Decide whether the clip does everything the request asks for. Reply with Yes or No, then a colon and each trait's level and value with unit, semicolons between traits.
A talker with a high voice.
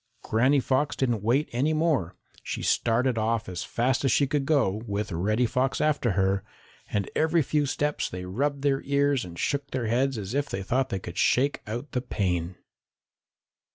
No: low, 125 Hz